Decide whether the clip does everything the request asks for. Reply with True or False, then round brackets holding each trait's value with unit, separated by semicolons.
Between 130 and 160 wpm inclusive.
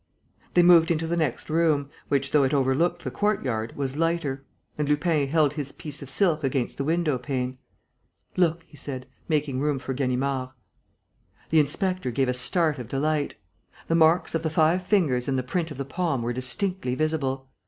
False (185 wpm)